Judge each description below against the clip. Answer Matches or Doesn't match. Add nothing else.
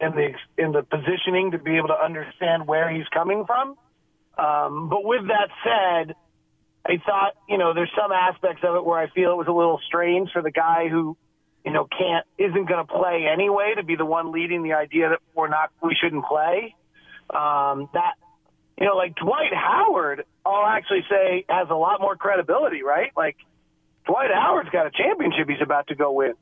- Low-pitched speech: Doesn't match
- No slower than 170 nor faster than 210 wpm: Matches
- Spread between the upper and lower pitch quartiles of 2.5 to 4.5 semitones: Matches